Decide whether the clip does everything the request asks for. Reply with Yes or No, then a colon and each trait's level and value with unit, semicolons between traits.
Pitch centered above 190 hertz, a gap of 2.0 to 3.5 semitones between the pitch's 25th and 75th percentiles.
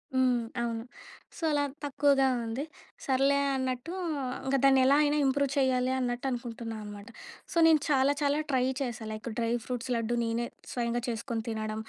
Yes: very high, 250 Hz; average, 2.9 semitones